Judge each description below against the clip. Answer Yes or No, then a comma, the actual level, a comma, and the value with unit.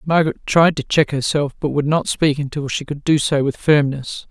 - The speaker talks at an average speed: No, fast, 225 wpm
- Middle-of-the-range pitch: Yes, medium, 145 Hz